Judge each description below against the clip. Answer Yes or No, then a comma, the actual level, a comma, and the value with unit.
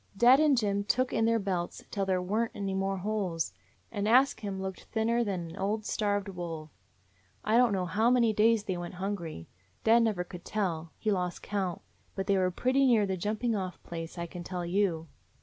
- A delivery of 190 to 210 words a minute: Yes, fast, 205 wpm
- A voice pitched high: Yes, high, 200 Hz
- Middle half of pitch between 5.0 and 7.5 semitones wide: No, average, 3.7 semitones